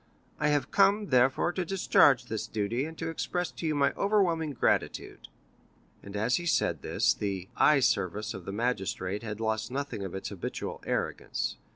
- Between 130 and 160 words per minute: No, average, 175 wpm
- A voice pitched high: No, low, 125 Hz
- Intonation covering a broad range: Yes, wide, 7.6 semitones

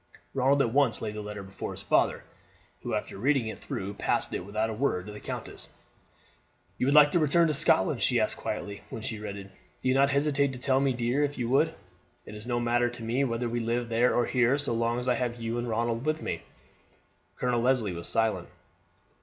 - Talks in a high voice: No, low, 120 Hz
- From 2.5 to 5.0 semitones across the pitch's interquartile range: Yes, average, 3.4 semitones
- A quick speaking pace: Yes, fast, 225 wpm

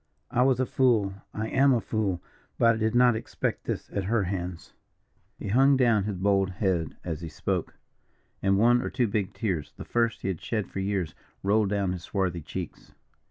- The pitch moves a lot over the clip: No, average, 3.8 semitones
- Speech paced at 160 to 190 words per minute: No, average, 200 wpm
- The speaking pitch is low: Yes, low, 100 Hz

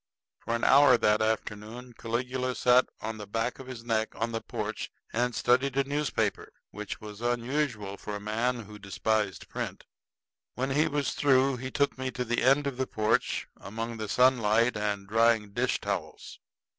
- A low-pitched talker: Yes, low, 115 Hz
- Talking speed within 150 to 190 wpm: Yes, average, 175 wpm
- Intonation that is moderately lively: Yes, average, 3.2 semitones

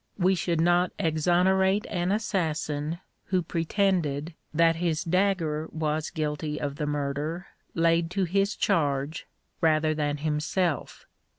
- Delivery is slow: Yes, slow, 120 wpm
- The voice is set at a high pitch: No, medium, 165 Hz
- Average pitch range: Yes, average, 3.1 semitones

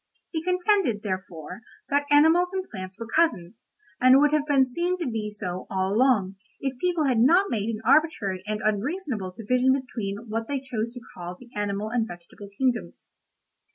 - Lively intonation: Yes, wide, 6.1 semitones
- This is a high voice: Yes, high, 235 Hz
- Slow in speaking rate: No, average, 175 wpm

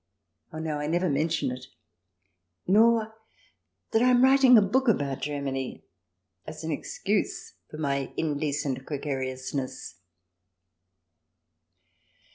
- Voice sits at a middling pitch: Yes, medium, 150 Hz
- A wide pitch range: Yes, wide, 6.9 semitones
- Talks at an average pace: No, slow, 105 wpm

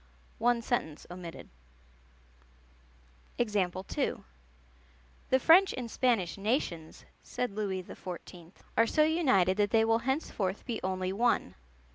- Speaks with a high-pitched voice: Yes, high, 210 Hz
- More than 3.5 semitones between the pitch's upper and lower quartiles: Yes, average, 4.7 semitones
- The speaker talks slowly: Yes, slow, 105 wpm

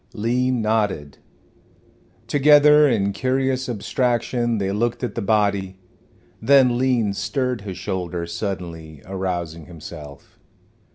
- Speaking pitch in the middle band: No, low, 105 Hz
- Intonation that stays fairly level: No, average, 5.3 semitones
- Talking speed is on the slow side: Yes, slow, 105 wpm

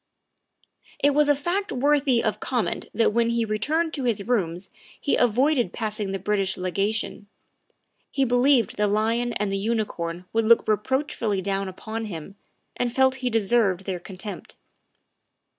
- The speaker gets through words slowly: No, average, 155 wpm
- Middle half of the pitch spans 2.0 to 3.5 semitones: No, average, 4.0 semitones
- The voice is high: Yes, high, 225 Hz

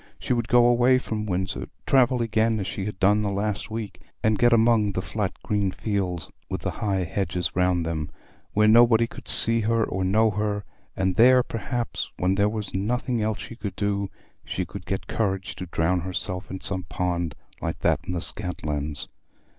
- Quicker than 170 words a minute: Yes, average, 185 wpm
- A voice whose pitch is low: Yes, low, 105 Hz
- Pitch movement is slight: No, average, 3.5 semitones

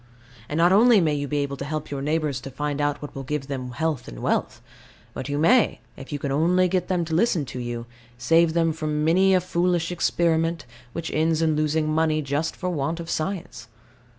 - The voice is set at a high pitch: No, medium, 155 Hz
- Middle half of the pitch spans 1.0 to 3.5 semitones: Yes, average, 2.9 semitones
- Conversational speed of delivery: No, fast, 215 wpm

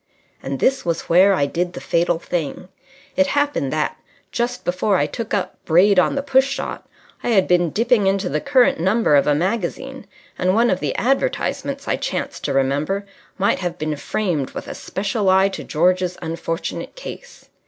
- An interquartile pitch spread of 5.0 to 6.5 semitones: Yes, wide, 5.6 semitones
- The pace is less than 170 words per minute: No, average, 185 wpm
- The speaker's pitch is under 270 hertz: Yes, medium, 185 Hz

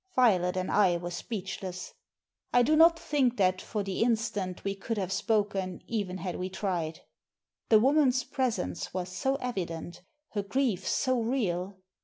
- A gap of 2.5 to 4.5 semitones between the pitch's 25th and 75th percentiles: No, average, 4.9 semitones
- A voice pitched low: No, high, 200 Hz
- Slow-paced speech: No, average, 155 wpm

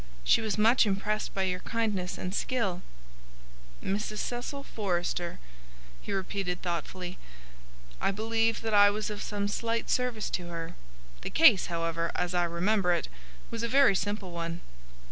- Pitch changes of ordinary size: Yes, average, 3.9 semitones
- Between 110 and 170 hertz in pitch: No, high, 200 Hz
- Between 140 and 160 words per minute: Yes, average, 150 wpm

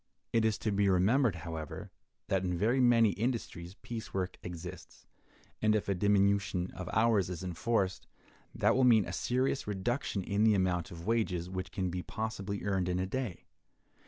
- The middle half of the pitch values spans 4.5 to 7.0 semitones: No, average, 3.6 semitones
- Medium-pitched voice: No, low, 100 Hz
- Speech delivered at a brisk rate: No, average, 175 wpm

